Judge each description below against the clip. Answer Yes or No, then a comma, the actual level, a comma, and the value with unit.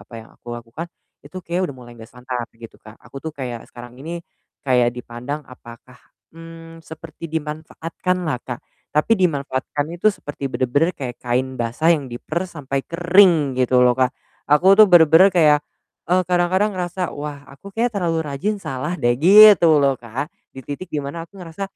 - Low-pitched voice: No, medium, 150 Hz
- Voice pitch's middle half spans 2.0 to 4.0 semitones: No, average, 5.2 semitones